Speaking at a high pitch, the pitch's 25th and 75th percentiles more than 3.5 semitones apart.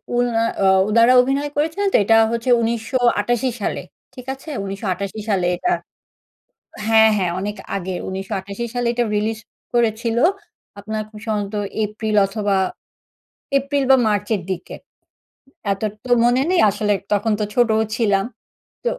No: high, 220 Hz; average, 3.1 semitones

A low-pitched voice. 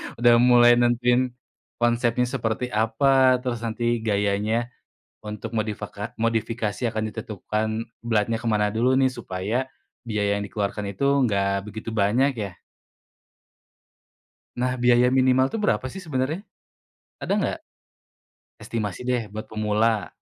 Yes: low, 115 Hz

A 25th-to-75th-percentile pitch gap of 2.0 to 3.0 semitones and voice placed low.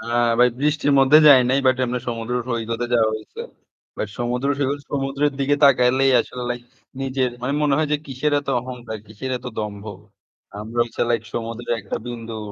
Yes: narrow, 2.6 semitones; low, 125 Hz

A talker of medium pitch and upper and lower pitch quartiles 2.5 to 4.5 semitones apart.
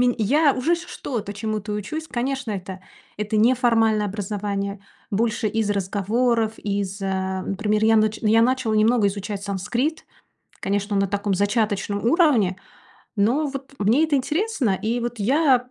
No: high, 215 Hz; average, 3.6 semitones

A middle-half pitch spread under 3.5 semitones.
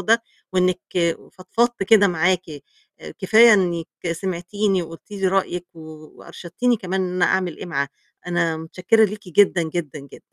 Yes: average, 2.9 semitones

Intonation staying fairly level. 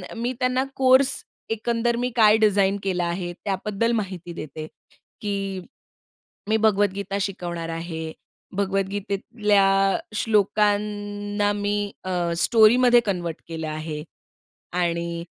No: average, 3.2 semitones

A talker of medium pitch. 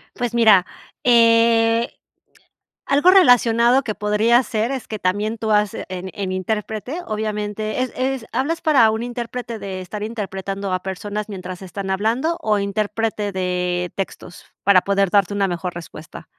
No: high, 210 Hz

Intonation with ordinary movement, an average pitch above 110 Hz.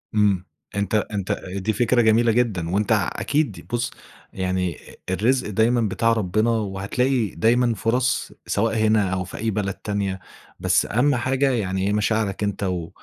No: average, 3.4 semitones; low, 105 Hz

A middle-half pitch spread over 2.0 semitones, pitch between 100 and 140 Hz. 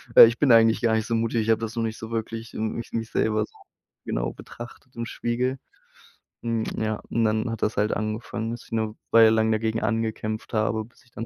No: narrow, 1.0 semitones; low, 115 Hz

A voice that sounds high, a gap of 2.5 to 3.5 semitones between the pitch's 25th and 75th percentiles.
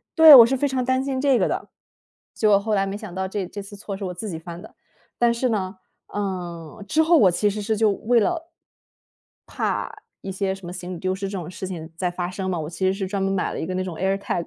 Yes: high, 195 Hz; average, 3.2 semitones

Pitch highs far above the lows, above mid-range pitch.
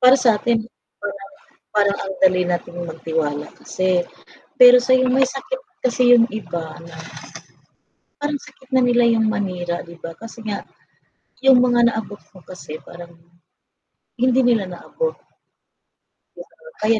Yes: wide, 5.9 semitones; high, 215 Hz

